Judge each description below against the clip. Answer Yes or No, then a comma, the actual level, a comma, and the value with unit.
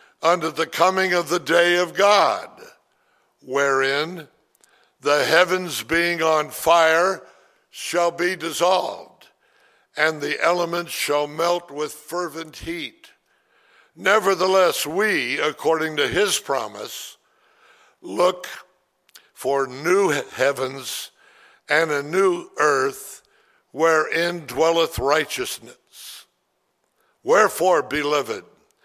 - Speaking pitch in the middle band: Yes, medium, 170 Hz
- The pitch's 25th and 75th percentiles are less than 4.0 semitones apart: Yes, average, 3.0 semitones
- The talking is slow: Yes, slow, 90 wpm